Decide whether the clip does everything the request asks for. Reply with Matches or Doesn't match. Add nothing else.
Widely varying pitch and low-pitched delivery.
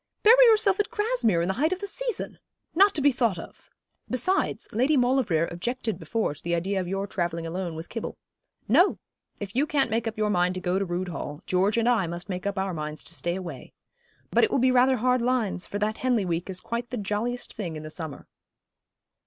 Doesn't match